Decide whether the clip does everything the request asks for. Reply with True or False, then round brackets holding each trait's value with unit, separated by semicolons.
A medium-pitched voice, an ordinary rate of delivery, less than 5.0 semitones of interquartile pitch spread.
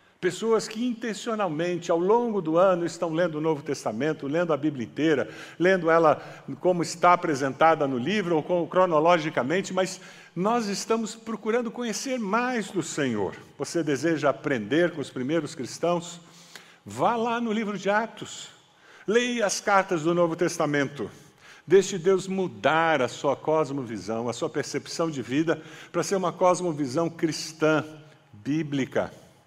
True (170 Hz; 145 wpm; 3.9 semitones)